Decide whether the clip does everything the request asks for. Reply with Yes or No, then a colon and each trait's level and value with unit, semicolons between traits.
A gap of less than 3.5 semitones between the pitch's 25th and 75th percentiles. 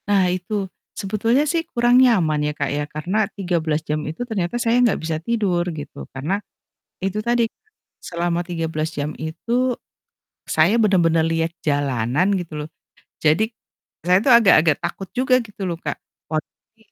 No: average, 5.2 semitones